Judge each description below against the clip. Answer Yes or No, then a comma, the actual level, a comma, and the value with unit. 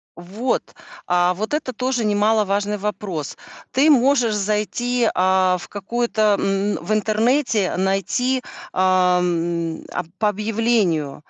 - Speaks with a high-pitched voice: Yes, high, 210 Hz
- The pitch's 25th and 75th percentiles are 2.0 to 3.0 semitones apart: No, average, 4.0 semitones